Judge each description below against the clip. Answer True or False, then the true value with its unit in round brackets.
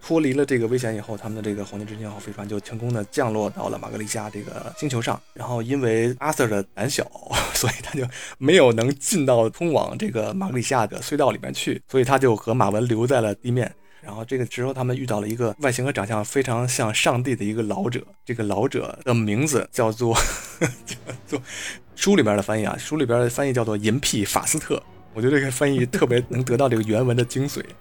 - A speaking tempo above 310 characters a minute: True (350 characters per minute)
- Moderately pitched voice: False (120 Hz)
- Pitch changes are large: False (3.6 semitones)